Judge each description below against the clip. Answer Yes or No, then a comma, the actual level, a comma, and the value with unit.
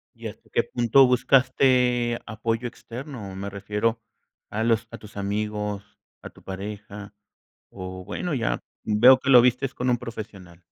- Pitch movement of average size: Yes, average, 3.4 semitones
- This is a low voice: Yes, low, 115 Hz